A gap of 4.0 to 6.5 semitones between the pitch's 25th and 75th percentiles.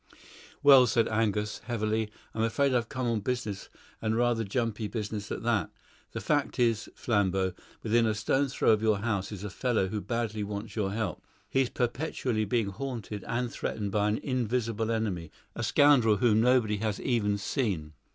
No: narrow, 2.6 semitones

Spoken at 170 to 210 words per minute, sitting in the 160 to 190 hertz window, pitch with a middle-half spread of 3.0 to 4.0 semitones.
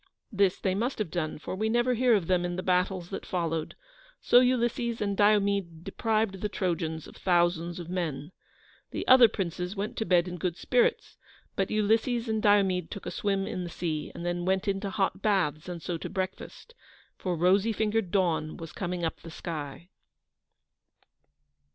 Yes: average, 180 wpm; medium, 185 Hz; average, 3.4 semitones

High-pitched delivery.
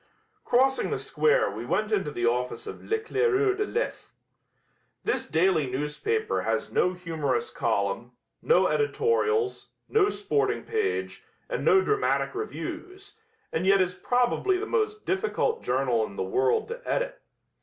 Yes: very high, 390 Hz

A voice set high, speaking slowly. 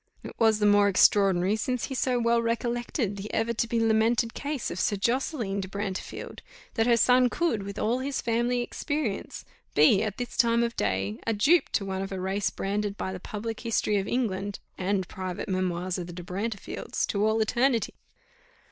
No: high, 215 Hz; average, 190 wpm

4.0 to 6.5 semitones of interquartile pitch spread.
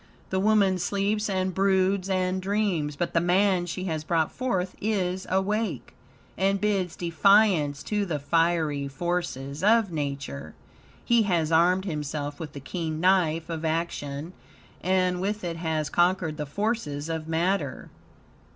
No: average, 3.6 semitones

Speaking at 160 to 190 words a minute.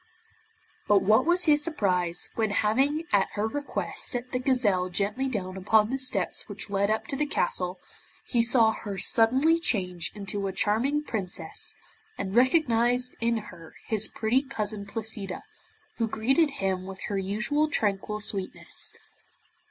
No: average, 150 wpm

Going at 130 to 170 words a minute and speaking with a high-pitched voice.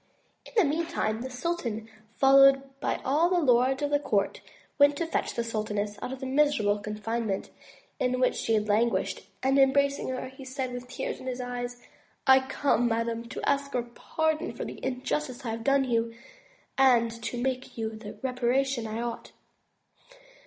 No: average, 180 wpm; very high, 255 Hz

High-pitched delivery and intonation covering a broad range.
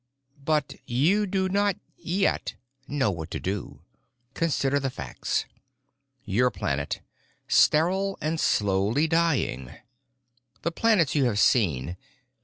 No: medium, 140 Hz; wide, 8.8 semitones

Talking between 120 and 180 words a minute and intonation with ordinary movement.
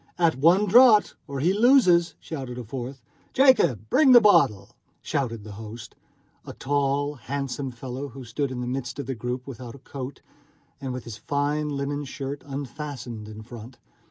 Yes: average, 170 wpm; average, 3.3 semitones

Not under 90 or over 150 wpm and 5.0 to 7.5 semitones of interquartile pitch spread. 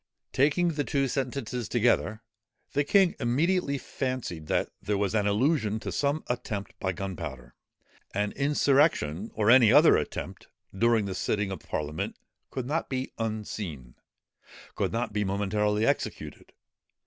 Yes: average, 140 wpm; average, 5.3 semitones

